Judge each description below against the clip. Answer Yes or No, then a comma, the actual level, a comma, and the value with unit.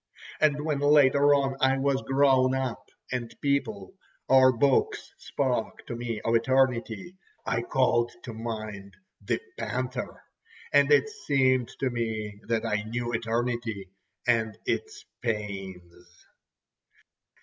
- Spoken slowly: Yes, slow, 120 wpm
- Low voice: Yes, low, 125 Hz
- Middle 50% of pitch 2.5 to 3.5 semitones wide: Yes, average, 3.2 semitones